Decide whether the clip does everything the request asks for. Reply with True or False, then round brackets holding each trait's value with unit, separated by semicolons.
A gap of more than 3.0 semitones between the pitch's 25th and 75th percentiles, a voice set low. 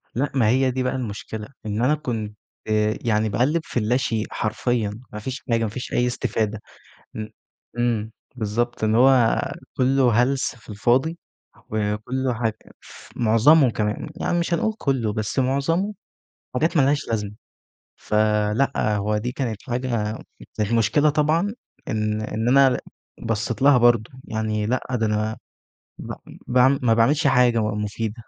True (3.5 semitones; 120 Hz)